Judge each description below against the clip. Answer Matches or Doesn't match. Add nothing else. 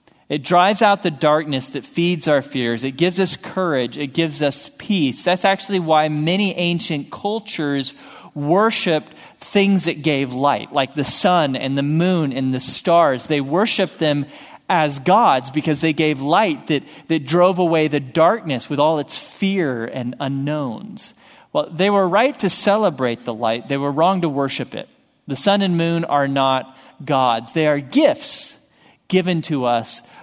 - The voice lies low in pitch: Doesn't match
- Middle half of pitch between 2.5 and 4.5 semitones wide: Doesn't match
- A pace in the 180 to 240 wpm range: Doesn't match